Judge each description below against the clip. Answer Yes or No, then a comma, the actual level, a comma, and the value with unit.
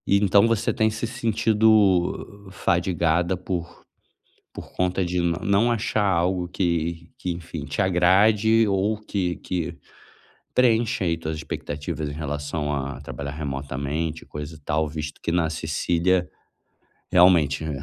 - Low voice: Yes, very low, 85 Hz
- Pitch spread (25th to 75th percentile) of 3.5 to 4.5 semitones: Yes, average, 4.0 semitones